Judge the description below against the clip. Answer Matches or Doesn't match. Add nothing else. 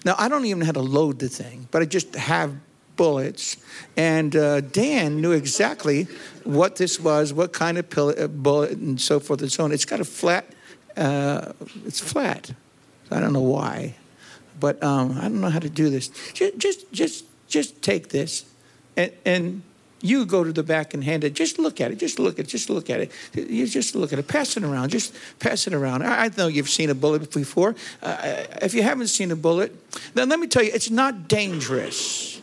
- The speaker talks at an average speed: Doesn't match